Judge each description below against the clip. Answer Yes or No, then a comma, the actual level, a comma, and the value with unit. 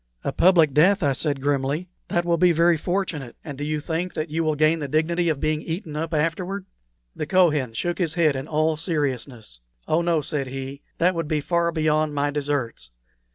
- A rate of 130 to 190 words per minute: No, average, 200 wpm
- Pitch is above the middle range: No, medium, 155 Hz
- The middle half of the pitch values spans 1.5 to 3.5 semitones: Yes, average, 2.8 semitones